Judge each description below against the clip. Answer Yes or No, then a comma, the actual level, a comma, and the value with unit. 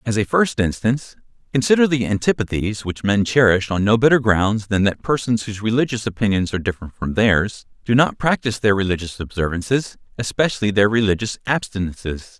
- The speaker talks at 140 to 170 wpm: Yes, average, 165 wpm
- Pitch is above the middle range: No, low, 110 Hz